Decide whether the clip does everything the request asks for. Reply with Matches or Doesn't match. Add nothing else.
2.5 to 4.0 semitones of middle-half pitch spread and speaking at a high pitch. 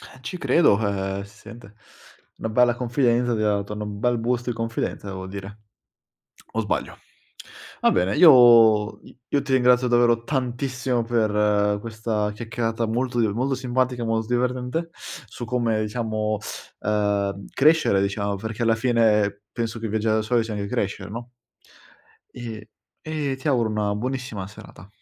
Doesn't match